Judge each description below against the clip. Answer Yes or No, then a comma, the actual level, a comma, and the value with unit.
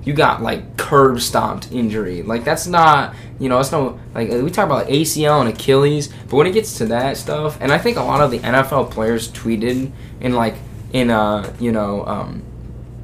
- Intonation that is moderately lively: Yes, average, 3.5 semitones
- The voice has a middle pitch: No, low, 125 Hz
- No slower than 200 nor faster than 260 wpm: Yes, fast, 205 wpm